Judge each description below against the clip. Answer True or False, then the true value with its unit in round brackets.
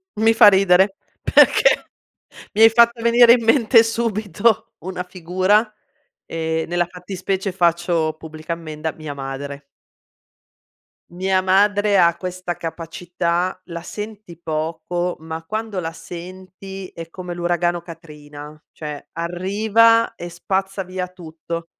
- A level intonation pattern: False (3.1 semitones)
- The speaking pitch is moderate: True (180 Hz)